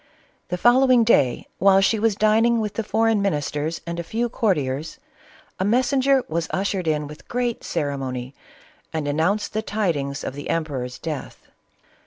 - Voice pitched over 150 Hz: Yes, high, 190 Hz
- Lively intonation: Yes, wide, 7.2 semitones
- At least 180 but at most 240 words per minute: No, average, 155 wpm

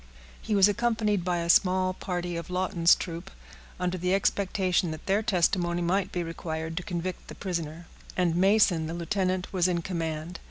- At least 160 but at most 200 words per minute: Yes, average, 170 wpm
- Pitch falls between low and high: Yes, medium, 180 Hz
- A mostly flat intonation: Yes, narrow, 1.9 semitones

